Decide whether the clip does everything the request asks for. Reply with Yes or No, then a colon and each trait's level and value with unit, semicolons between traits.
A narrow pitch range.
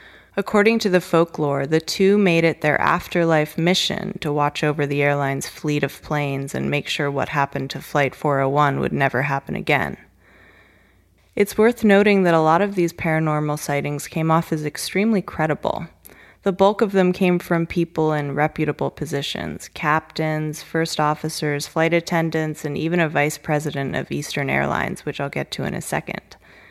No: average, 3.2 semitones